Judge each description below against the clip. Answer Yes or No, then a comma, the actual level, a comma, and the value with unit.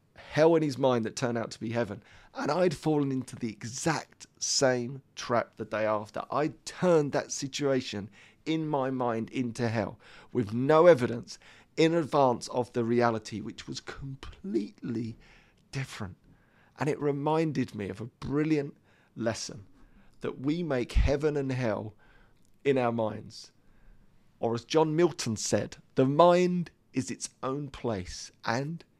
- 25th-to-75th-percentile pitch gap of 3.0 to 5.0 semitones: Yes, average, 4.5 semitones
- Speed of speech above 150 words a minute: No, average, 145 wpm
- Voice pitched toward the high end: No, low, 125 Hz